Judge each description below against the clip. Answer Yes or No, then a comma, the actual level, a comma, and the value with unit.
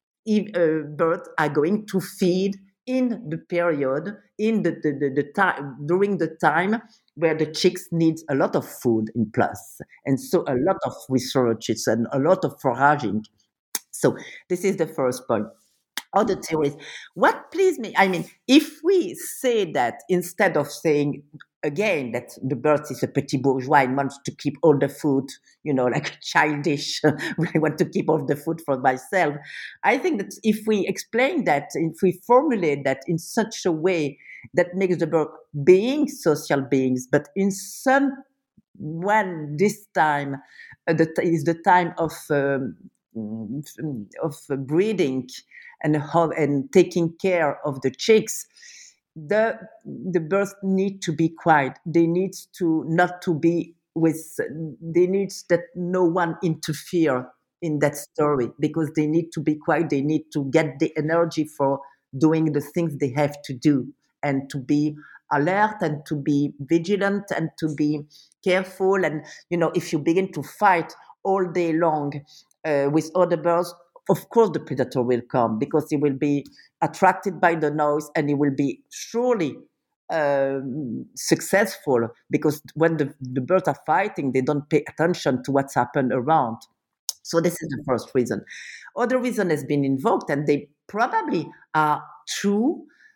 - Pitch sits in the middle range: Yes, medium, 160 Hz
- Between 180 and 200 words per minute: No, average, 165 wpm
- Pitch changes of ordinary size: Yes, average, 4.3 semitones